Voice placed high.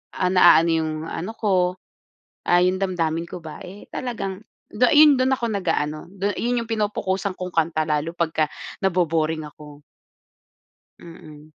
No: medium, 180 Hz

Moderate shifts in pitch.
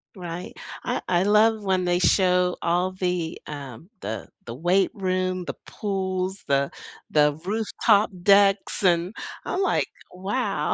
No: narrow, 2.2 semitones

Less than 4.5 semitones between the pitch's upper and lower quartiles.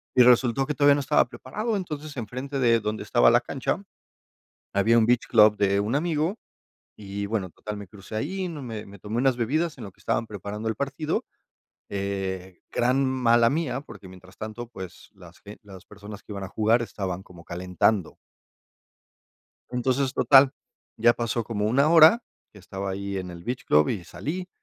No: average, 5.2 semitones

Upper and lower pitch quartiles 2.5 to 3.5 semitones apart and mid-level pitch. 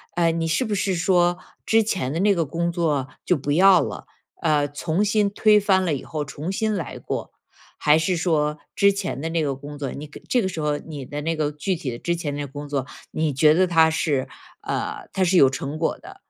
No: average, 4.2 semitones; medium, 165 Hz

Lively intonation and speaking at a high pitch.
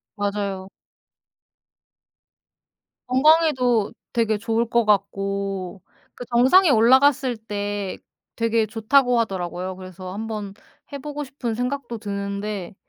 No: average, 3.8 semitones; high, 220 Hz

